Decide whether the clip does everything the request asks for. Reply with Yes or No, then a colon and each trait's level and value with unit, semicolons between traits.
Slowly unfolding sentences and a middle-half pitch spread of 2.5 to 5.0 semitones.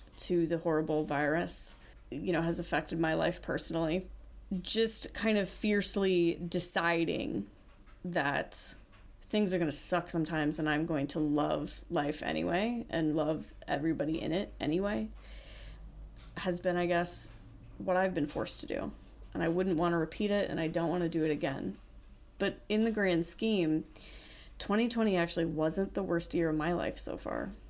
No: average, 160 wpm; average, 3.0 semitones